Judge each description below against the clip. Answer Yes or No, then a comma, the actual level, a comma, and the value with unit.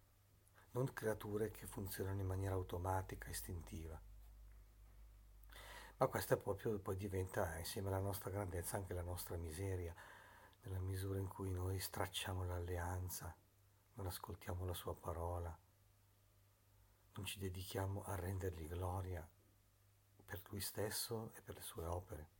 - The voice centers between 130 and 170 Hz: No, very low, 95 Hz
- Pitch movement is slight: Yes, narrow, 1.8 semitones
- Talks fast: No, average, 125 wpm